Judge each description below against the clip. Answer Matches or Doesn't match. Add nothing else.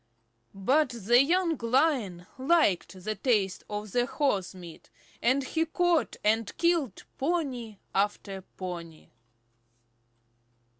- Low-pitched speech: Doesn't match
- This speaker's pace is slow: Matches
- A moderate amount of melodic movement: Doesn't match